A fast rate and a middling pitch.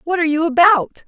No: fast, 225 wpm; very high, 325 Hz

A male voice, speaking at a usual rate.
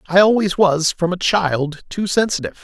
Yes: male; average, 180 wpm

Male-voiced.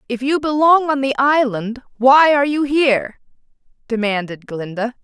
No: female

